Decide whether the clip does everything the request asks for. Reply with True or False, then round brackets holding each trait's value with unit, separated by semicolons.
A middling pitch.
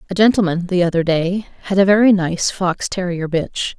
True (180 Hz)